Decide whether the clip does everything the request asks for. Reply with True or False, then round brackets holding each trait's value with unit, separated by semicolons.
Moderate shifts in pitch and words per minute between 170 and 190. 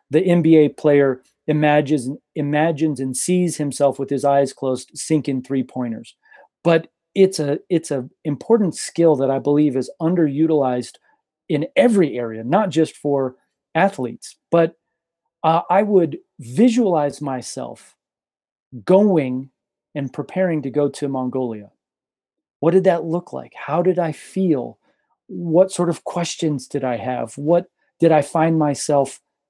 False (4.0 semitones; 140 wpm)